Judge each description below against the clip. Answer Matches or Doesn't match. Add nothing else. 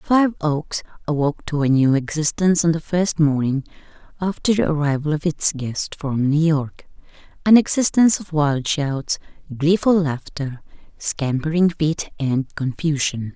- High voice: Doesn't match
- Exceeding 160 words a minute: Doesn't match